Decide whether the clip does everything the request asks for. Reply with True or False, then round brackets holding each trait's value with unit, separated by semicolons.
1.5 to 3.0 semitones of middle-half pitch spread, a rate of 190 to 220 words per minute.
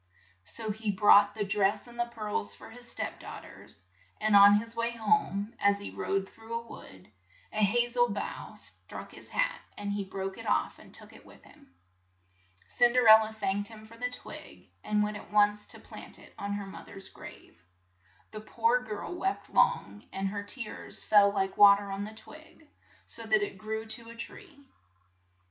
True (2.4 semitones; 195 wpm)